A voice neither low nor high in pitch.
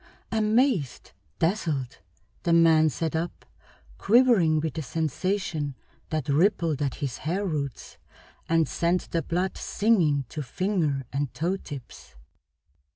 Yes: medium, 160 Hz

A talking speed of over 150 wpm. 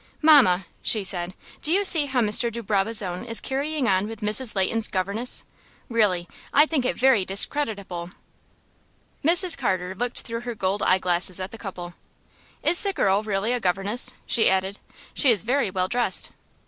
Yes: average, 170 wpm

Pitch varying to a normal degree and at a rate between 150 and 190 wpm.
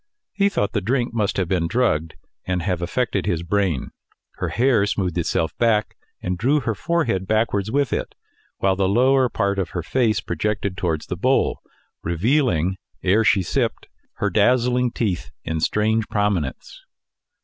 Yes: average, 5.0 semitones; average, 160 wpm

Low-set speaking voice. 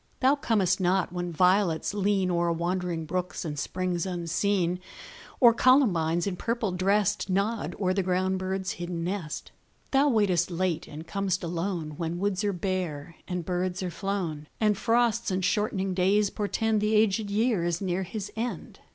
No: medium, 185 Hz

